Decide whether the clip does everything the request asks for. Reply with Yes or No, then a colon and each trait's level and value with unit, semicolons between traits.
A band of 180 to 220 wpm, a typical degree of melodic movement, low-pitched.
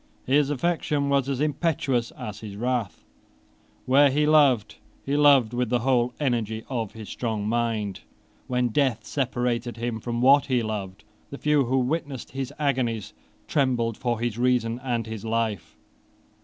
No: average, 155 wpm; average, 3.3 semitones; low, 125 Hz